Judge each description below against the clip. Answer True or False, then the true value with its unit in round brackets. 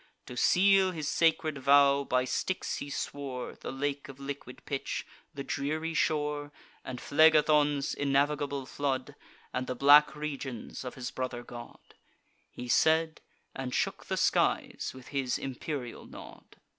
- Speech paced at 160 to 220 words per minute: False (140 wpm)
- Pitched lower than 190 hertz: True (140 Hz)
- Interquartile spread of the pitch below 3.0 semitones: True (2.4 semitones)